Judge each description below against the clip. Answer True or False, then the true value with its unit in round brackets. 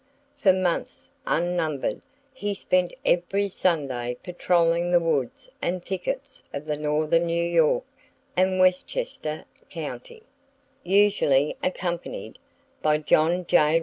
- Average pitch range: True (3.2 semitones)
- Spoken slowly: True (105 wpm)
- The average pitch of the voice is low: False (175 Hz)